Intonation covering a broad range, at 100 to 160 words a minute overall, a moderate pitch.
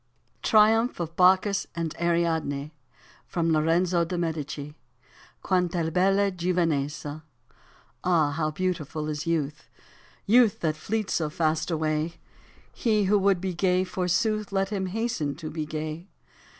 No: average, 3.5 semitones; average, 140 wpm; medium, 170 Hz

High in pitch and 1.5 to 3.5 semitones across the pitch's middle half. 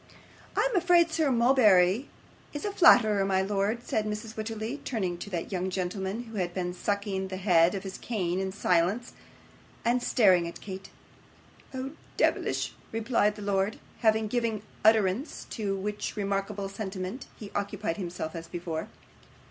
Yes: high, 205 Hz; average, 3.1 semitones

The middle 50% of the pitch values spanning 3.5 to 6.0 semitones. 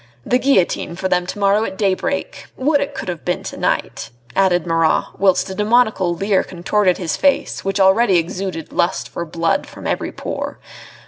No: average, 3.1 semitones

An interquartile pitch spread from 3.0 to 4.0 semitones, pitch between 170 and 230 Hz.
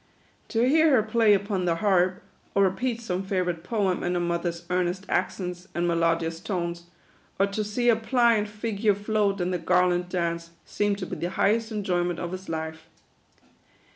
Yes: average, 3.3 semitones; medium, 185 Hz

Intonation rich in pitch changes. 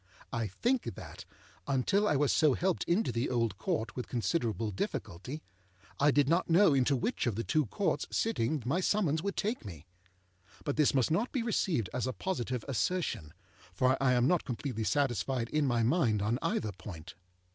Yes: wide, 6.4 semitones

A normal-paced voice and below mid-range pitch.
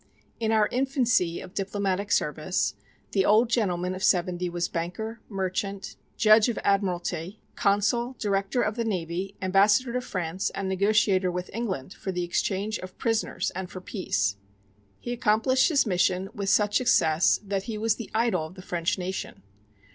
No: average, 160 wpm; high, 195 Hz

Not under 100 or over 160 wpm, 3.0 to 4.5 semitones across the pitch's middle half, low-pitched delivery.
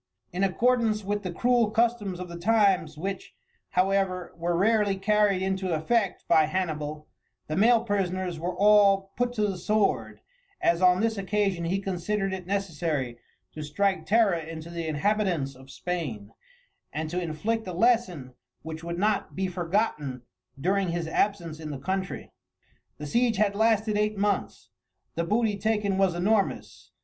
No: average, 155 wpm; average, 3.7 semitones; high, 190 Hz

